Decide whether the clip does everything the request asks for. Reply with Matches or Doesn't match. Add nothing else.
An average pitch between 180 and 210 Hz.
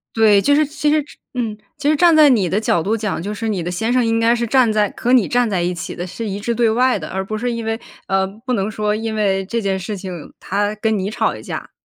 Doesn't match